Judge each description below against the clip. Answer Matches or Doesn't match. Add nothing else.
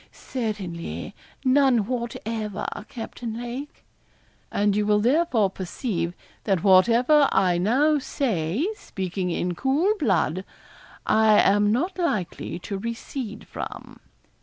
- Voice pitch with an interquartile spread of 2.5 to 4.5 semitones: Doesn't match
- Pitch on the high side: Matches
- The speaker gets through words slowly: Matches